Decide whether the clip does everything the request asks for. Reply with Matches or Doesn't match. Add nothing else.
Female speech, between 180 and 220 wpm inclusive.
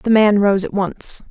Doesn't match